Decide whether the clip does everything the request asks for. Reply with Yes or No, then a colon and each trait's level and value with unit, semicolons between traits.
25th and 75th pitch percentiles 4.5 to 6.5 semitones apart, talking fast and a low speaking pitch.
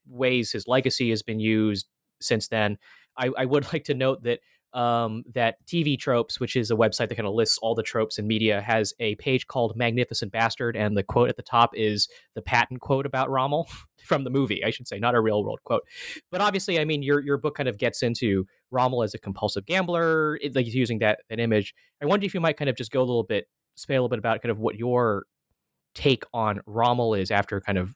No: average, 3.1 semitones; fast, 240 wpm; low, 120 Hz